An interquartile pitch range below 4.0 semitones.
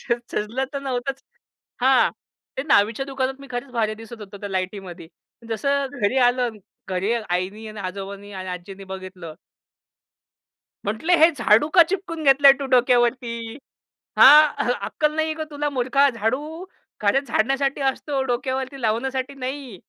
No: average, 4.6 semitones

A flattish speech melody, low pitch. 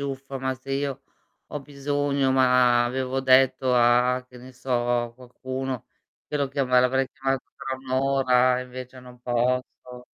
Yes: narrow, 1.1 semitones; low, 130 Hz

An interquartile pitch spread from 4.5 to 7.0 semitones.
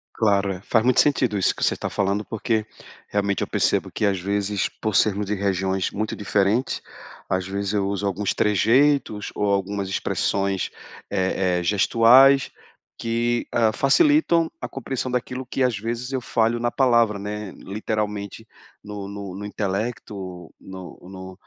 No: average, 3.1 semitones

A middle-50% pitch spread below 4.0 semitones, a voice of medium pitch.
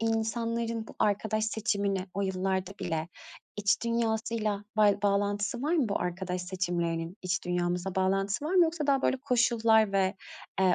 No: average, 3.4 semitones; high, 205 Hz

